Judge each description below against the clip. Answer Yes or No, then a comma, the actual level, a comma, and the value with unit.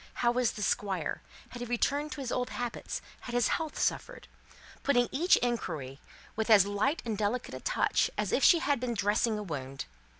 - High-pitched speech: Yes, high, 235 Hz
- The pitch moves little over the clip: No, average, 3.6 semitones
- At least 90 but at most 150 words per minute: No, average, 195 wpm